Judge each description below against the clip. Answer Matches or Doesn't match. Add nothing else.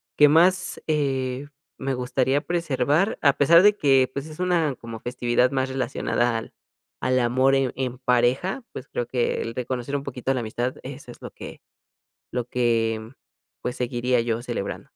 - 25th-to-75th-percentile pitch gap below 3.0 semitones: Matches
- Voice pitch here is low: Matches